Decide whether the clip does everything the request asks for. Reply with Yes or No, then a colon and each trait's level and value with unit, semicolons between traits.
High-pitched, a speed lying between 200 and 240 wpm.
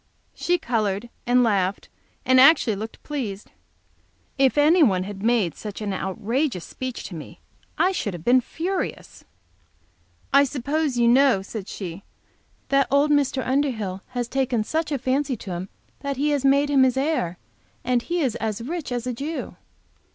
No: very high, 255 Hz; average, 165 wpm